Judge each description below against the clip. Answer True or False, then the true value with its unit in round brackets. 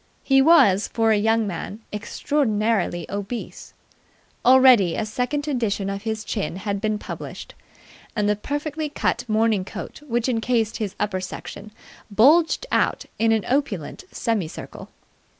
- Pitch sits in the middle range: False (220 Hz)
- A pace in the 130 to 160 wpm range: True (140 wpm)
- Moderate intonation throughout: True (3.7 semitones)